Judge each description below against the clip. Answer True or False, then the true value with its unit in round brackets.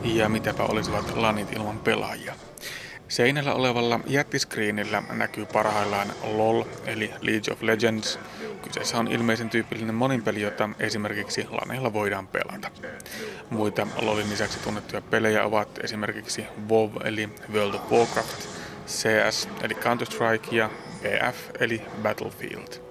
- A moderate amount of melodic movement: False (1.6 semitones)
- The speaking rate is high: False (120 wpm)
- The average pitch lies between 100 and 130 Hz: True (110 Hz)